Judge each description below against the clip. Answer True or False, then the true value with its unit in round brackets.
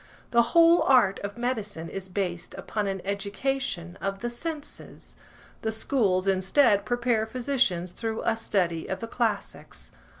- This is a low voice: False (215 Hz)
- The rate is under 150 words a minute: True (140 wpm)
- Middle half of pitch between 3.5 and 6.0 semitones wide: True (4.1 semitones)